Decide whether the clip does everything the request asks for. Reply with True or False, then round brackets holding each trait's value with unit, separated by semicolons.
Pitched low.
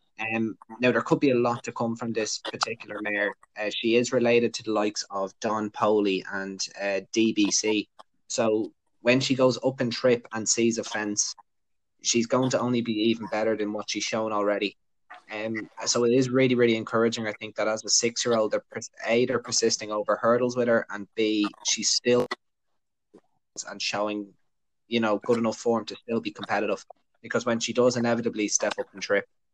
True (110 Hz)